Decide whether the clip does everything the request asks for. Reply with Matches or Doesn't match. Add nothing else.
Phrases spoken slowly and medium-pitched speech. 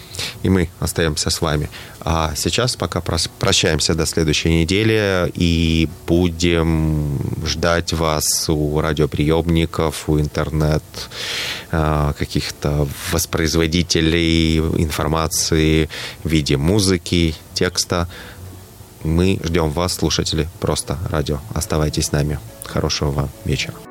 Doesn't match